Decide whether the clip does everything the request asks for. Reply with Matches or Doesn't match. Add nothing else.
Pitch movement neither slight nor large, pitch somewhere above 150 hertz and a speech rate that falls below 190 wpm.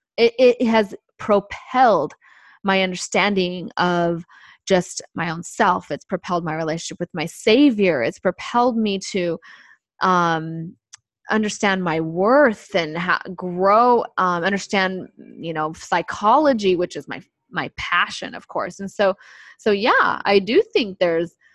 Matches